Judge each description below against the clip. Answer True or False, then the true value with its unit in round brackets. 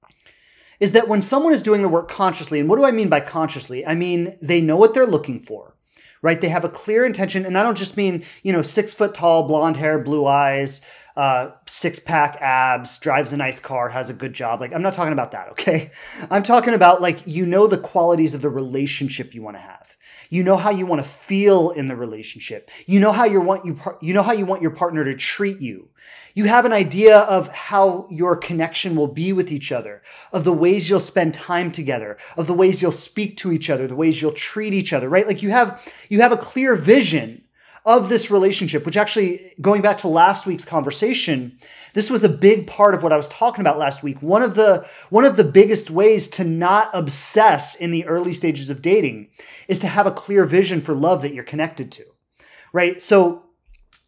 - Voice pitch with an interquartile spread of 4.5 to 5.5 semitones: True (4.9 semitones)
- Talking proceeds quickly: True (225 wpm)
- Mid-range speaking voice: True (175 Hz)